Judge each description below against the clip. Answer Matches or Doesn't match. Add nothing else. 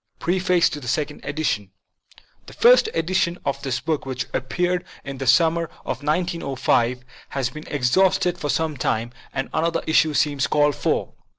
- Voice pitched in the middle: Matches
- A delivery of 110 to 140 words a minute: Doesn't match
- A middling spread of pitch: Matches